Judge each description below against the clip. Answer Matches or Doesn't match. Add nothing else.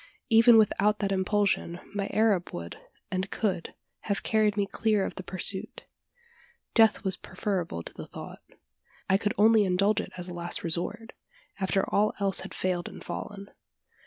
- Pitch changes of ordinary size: Doesn't match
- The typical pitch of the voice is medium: Doesn't match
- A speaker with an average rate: Matches